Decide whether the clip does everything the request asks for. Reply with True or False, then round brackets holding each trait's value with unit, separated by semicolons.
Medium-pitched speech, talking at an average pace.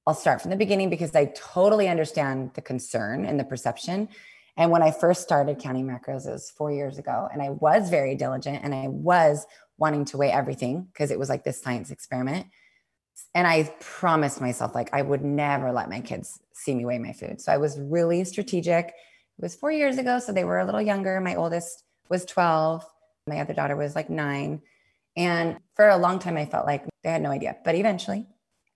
False (160 Hz; 210 wpm)